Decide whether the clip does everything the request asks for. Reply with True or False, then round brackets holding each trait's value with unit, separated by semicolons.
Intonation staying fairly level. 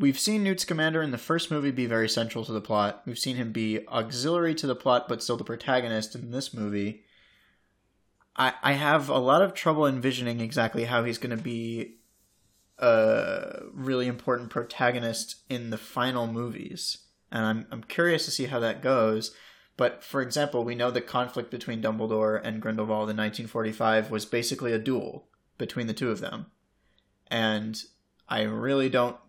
False (3.2 semitones)